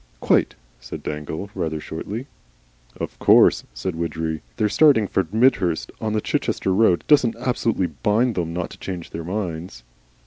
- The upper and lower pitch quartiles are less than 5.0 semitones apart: No, average, 5.3 semitones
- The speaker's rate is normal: Yes, average, 150 wpm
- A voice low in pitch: Yes, very low, 95 Hz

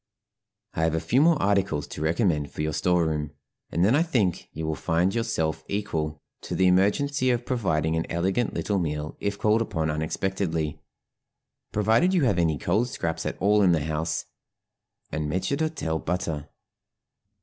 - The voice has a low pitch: Yes, very low, 90 Hz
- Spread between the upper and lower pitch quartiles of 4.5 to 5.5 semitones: Yes, average, 5.2 semitones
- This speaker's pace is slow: No, average, 170 wpm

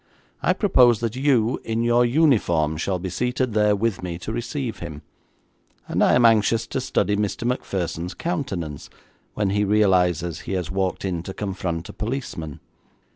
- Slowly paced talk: No, average, 165 wpm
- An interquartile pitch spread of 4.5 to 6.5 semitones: Yes, average, 5.0 semitones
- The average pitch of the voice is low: Yes, low, 105 Hz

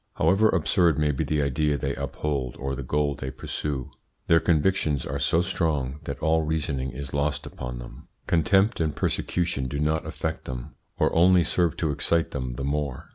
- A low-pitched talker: Yes, very low, 75 Hz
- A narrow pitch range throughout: No, average, 3.2 semitones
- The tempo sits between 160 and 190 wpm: Yes, average, 185 wpm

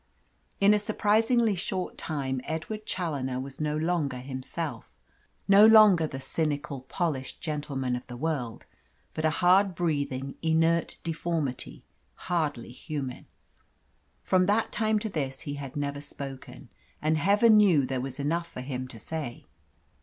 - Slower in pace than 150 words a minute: Yes, average, 140 wpm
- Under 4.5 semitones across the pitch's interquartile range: No, average, 5.0 semitones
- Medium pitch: Yes, medium, 155 Hz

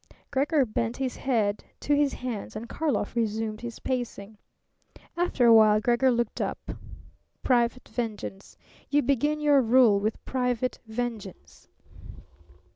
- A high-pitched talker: Yes, high, 240 Hz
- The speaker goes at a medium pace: No, slow, 125 wpm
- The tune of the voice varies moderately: Yes, average, 3.3 semitones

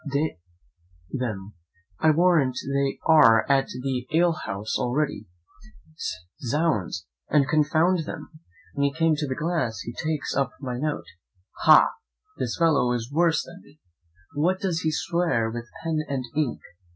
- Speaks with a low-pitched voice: No, medium, 145 Hz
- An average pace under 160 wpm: Yes, average, 145 wpm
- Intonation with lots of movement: No, average, 4.4 semitones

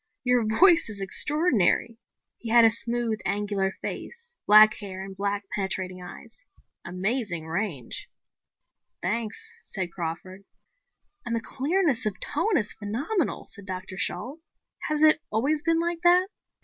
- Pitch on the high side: Yes, high, 220 Hz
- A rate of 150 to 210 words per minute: No, slow, 135 wpm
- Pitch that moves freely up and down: Yes, wide, 7.5 semitones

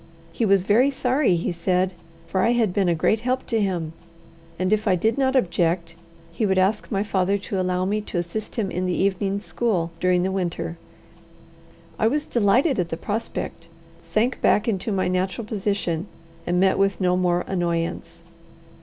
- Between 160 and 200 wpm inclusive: Yes, average, 180 wpm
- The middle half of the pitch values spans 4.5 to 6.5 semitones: No, average, 3.2 semitones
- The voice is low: No, high, 190 Hz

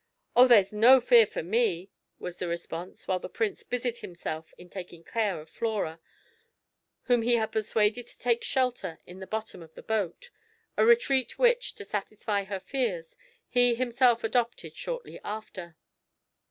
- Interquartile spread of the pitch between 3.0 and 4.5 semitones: No, average, 5.0 semitones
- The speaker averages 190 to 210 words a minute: No, average, 160 wpm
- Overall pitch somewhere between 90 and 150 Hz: No, high, 220 Hz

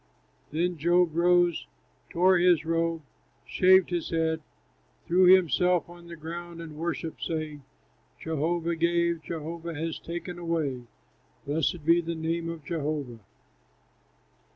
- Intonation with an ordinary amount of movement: No, narrow, 1.3 semitones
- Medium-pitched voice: Yes, medium, 170 Hz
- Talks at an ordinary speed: No, slow, 120 wpm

